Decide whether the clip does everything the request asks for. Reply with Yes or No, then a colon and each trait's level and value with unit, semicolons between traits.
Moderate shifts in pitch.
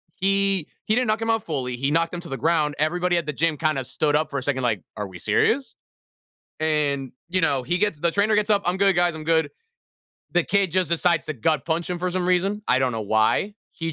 Yes: average, 4.5 semitones